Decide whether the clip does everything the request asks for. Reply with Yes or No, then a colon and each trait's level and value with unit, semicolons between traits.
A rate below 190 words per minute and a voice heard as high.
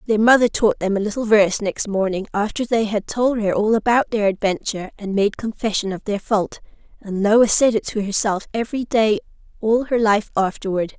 No: average, 195 wpm; high, 210 Hz